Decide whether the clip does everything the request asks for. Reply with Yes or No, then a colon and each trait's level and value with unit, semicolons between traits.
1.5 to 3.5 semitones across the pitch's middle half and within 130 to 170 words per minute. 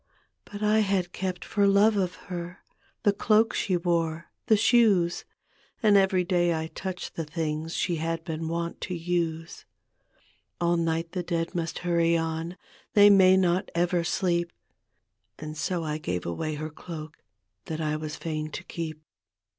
Yes: narrow, 2.5 semitones; average, 160 wpm